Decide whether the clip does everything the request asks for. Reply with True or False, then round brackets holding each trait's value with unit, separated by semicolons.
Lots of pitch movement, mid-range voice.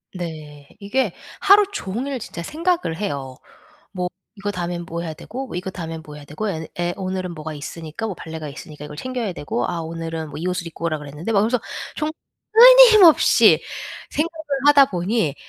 True (6.9 semitones; 175 Hz)